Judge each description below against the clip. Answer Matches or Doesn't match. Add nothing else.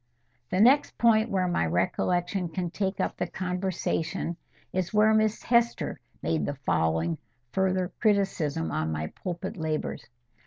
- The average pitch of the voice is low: Doesn't match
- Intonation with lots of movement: Matches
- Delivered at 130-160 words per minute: Matches